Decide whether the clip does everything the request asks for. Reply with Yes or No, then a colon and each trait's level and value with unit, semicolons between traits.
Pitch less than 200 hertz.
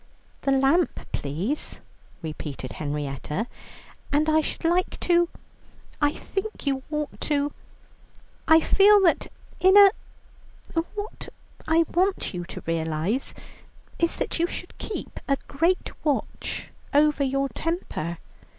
No: very high, 295 Hz